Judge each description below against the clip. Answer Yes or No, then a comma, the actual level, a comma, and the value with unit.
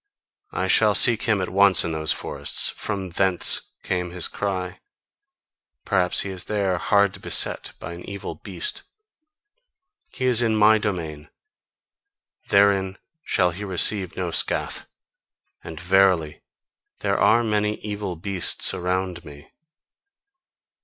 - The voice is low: Yes, very low, 95 Hz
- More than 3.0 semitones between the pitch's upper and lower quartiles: No, narrow, 2.6 semitones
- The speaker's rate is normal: No, slow, 125 wpm